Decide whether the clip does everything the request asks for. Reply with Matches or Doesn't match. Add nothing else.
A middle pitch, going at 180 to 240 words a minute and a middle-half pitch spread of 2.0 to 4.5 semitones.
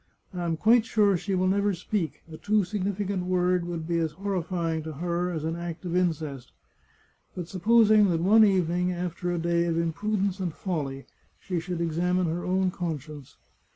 Matches